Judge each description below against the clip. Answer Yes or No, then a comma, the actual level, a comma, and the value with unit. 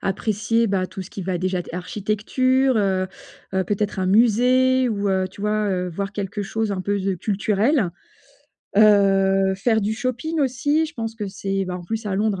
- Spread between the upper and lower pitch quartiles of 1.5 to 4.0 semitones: Yes, average, 2.9 semitones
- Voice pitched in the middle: No, high, 205 Hz